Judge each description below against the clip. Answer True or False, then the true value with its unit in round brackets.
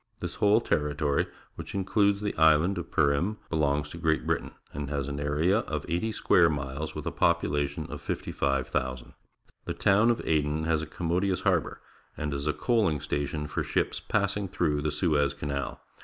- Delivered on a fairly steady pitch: False (3.9 semitones)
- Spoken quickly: False (175 wpm)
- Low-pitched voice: True (75 Hz)